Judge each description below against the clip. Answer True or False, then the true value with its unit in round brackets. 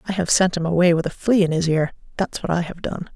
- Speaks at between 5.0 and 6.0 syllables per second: False (6.2 syllables/s)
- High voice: False (175 Hz)